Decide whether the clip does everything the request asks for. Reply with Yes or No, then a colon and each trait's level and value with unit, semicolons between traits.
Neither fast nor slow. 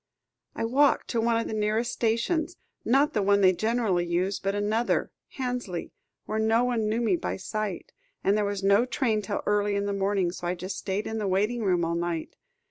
No: fast, 210 wpm